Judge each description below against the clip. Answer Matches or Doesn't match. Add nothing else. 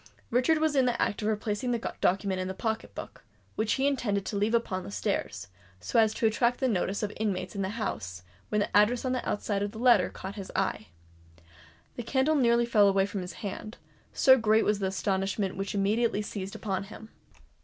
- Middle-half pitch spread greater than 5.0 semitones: Doesn't match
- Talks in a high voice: Matches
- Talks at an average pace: Doesn't match